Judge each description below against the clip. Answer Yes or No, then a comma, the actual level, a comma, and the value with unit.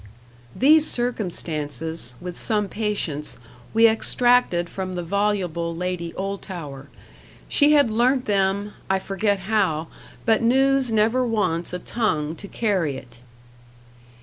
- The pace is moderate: No, slow, 120 wpm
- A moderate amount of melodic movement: Yes, average, 5.0 semitones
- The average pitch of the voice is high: Yes, high, 195 Hz